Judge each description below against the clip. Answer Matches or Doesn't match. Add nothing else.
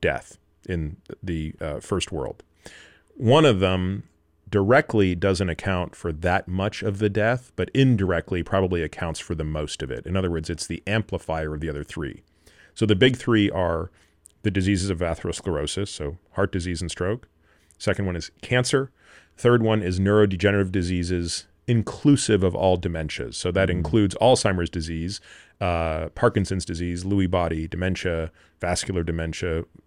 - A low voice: Matches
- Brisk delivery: Doesn't match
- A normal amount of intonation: Matches